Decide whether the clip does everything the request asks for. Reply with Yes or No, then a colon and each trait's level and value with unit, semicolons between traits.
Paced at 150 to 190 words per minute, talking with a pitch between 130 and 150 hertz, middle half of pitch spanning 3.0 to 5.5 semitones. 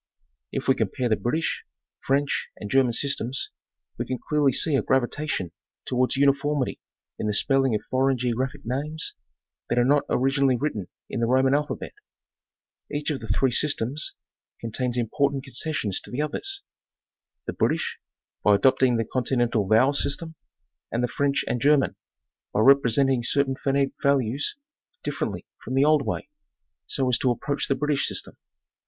No: average, 160 wpm; low, 135 Hz; narrow, 2.6 semitones